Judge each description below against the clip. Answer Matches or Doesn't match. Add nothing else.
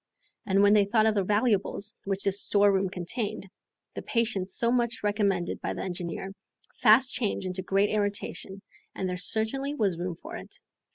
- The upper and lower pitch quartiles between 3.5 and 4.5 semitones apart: Doesn't match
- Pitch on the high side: Matches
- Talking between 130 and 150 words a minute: Doesn't match